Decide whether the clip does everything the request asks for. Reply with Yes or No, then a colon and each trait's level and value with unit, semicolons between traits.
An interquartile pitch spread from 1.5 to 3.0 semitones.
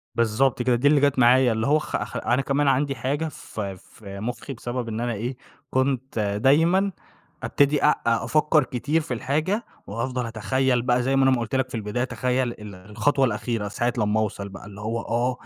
No: average, 3.4 semitones